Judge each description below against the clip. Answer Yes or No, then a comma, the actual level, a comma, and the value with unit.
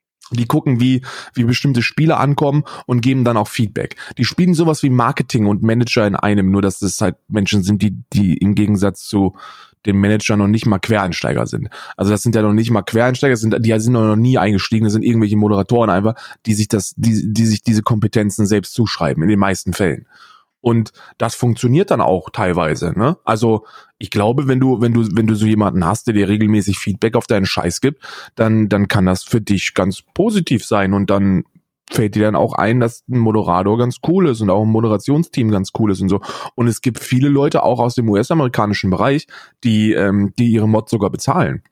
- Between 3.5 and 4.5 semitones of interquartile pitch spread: No, average, 3.0 semitones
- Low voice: Yes, low, 110 Hz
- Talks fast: Yes, fast, 210 wpm